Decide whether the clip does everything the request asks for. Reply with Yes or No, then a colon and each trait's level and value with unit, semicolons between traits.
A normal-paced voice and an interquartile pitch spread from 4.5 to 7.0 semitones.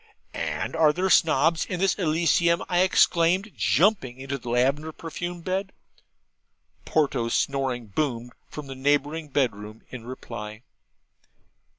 No: slow, 125 wpm; average, 5.3 semitones